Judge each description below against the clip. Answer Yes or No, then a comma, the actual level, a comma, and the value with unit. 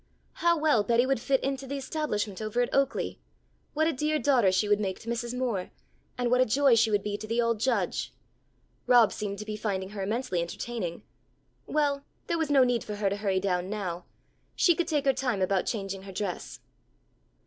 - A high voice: Yes, high, 230 Hz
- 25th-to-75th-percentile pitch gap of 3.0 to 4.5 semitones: No, average, 5.1 semitones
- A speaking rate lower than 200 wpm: No, fast, 205 wpm